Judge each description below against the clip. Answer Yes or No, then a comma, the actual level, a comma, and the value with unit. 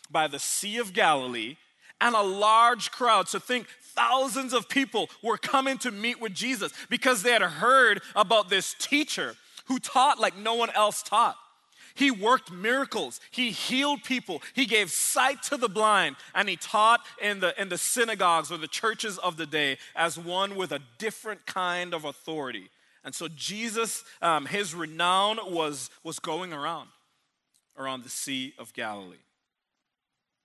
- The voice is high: Yes, high, 210 Hz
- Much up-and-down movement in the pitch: Yes, wide, 6.2 semitones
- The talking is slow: No, average, 165 wpm